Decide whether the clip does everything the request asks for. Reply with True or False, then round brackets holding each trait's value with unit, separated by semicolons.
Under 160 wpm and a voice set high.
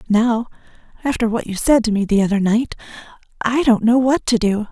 False (205 wpm; 225 Hz)